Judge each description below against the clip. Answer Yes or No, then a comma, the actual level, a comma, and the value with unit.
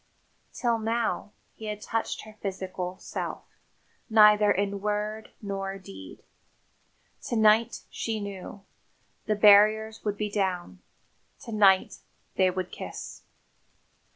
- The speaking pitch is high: Yes, high, 210 Hz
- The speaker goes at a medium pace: No, slow, 115 wpm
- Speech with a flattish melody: Yes, narrow, 2.0 semitones